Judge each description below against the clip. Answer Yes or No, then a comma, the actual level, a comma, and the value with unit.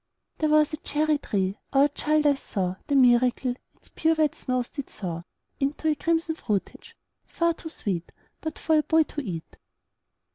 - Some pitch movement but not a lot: Yes, average, 4.6 semitones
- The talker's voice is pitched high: Yes, very high, 290 Hz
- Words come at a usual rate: Yes, average, 175 wpm